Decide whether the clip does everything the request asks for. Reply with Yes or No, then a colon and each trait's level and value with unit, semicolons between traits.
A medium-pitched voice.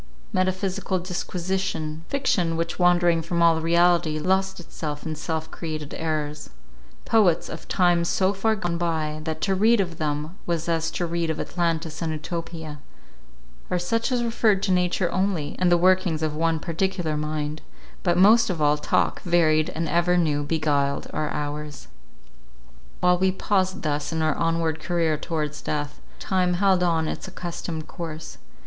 Yes: medium, 170 Hz